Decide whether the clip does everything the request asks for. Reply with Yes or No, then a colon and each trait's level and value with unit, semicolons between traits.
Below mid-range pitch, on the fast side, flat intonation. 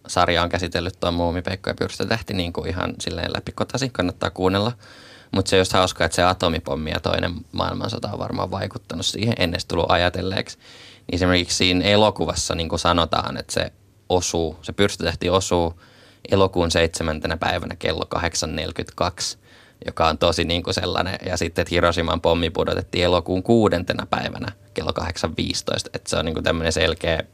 Yes: very low, 90 Hz; fast, 160 wpm; narrow, 2.2 semitones